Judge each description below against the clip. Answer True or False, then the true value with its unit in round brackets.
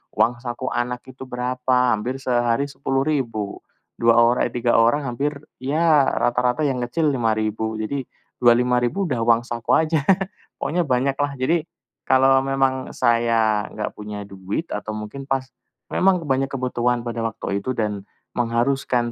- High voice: False (125 Hz)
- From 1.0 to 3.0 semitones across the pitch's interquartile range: True (2.7 semitones)